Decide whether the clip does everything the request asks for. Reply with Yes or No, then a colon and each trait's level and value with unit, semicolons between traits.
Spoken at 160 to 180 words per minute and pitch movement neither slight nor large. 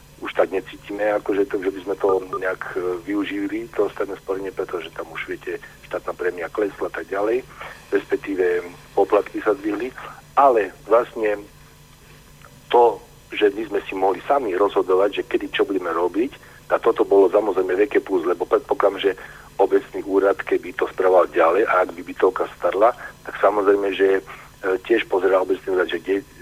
Yes: fast, 165 wpm; average, 4.1 semitones